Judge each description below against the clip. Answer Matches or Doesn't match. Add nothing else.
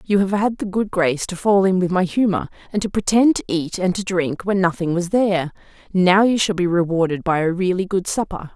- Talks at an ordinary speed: Doesn't match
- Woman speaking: Matches